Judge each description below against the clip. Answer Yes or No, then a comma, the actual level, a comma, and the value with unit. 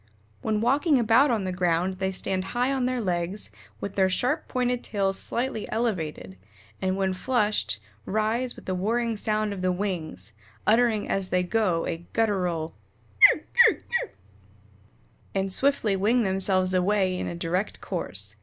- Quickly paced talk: No, average, 155 wpm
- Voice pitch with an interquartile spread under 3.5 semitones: No, average, 4.0 semitones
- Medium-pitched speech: No, high, 200 Hz